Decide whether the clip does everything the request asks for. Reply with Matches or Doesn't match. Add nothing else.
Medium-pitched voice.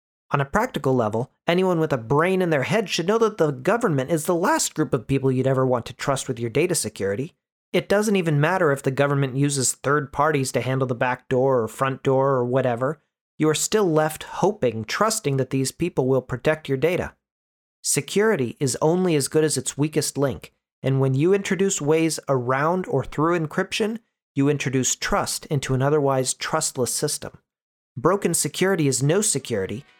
Matches